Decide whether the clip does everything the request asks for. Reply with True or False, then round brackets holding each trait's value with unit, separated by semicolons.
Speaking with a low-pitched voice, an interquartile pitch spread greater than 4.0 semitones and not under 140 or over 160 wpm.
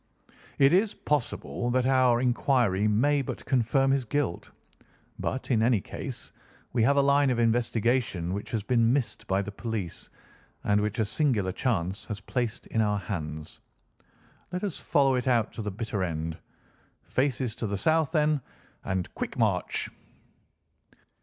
True (120 Hz; 4.7 semitones; 155 wpm)